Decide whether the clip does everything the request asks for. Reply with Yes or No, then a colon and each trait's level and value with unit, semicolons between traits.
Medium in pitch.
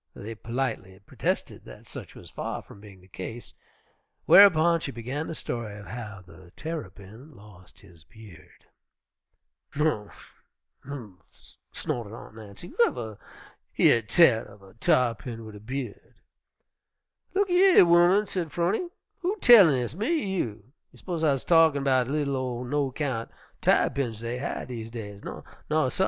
No: low, 125 Hz